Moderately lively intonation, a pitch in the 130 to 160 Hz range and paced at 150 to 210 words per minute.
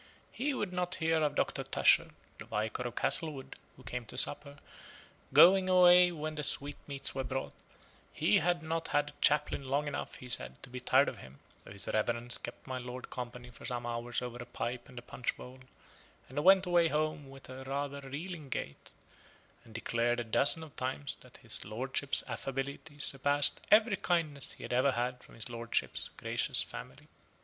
Yes: average, 4.1 semitones; low, 135 Hz; average, 185 wpm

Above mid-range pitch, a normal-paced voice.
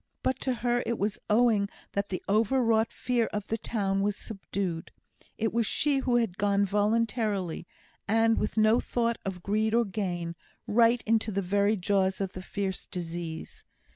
Yes: high, 210 Hz; average, 170 wpm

